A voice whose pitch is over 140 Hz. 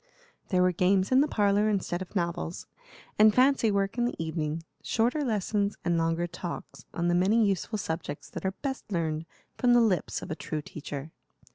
Yes: high, 190 Hz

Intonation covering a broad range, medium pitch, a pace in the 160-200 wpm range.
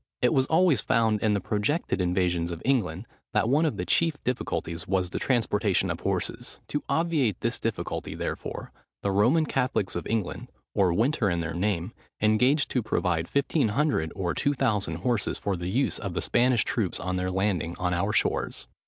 No: wide, 6.0 semitones; low, 105 Hz; average, 180 wpm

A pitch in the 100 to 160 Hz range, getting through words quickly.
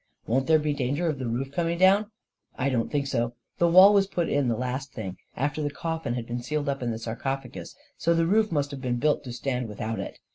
Yes: low, 135 Hz; fast, 250 wpm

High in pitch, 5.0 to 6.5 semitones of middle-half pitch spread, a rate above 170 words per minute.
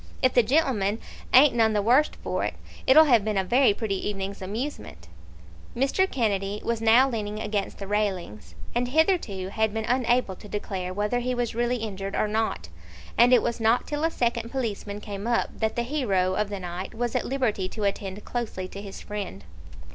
No: high, 220 Hz; average, 3.7 semitones; average, 195 wpm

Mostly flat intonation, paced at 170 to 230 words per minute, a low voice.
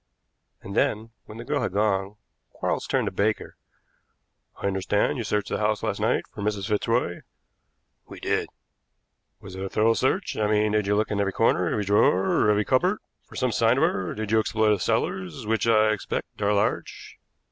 Yes: narrow, 1.9 semitones; average, 190 wpm; low, 105 Hz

